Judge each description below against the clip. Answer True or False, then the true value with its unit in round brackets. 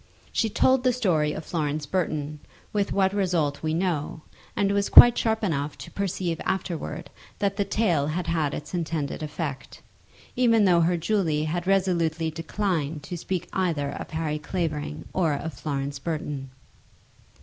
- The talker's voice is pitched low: False (165 Hz)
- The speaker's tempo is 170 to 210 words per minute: False (155 wpm)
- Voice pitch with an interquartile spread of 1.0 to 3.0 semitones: False (4.1 semitones)